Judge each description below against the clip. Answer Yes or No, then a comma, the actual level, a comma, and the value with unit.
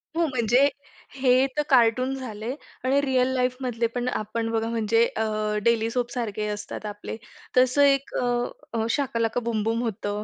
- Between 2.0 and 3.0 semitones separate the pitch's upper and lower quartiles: Yes, narrow, 2.4 semitones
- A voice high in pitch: Yes, high, 235 Hz